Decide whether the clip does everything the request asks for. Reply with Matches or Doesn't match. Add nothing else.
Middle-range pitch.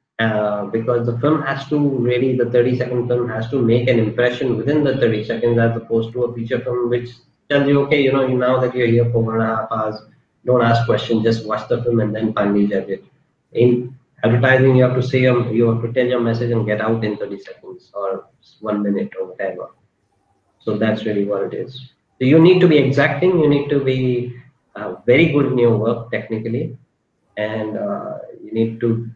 Doesn't match